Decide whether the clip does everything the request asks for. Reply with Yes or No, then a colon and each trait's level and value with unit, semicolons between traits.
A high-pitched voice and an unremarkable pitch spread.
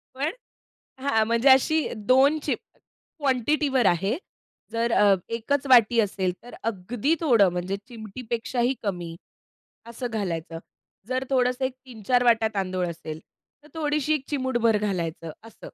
Yes: high, 235 Hz; average, 4.7 semitones